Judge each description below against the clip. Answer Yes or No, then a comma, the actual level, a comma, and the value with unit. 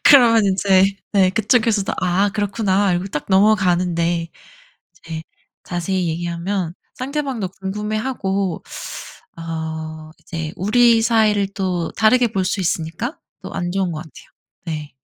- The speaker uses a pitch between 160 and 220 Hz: Yes, high, 190 Hz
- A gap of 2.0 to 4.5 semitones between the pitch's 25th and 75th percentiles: Yes, average, 3.9 semitones